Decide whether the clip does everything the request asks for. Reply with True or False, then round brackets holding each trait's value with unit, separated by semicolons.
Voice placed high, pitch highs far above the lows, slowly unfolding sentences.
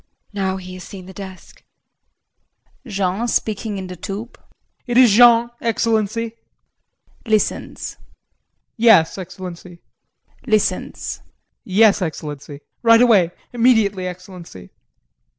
False (200 Hz; 3.8 semitones; 100 wpm)